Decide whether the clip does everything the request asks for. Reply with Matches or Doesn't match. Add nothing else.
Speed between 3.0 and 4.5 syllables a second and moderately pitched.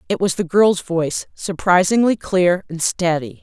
Matches